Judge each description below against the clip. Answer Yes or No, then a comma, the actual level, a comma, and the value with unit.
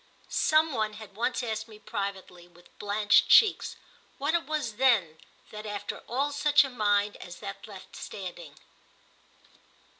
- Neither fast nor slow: Yes, average, 145 wpm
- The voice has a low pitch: No, high, 215 Hz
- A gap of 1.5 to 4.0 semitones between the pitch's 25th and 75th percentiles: No, average, 4.7 semitones